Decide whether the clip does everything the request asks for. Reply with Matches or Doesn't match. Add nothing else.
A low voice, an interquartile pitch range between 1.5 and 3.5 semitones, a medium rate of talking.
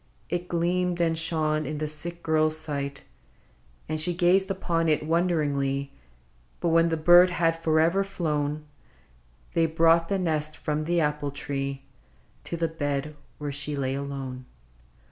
Doesn't match